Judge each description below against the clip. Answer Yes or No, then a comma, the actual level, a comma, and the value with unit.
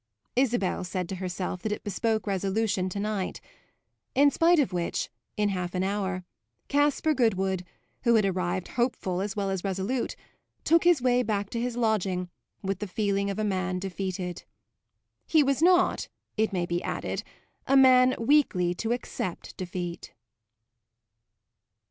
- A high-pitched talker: Yes, high, 200 Hz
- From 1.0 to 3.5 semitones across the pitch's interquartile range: No, average, 4.7 semitones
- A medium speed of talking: Yes, average, 150 wpm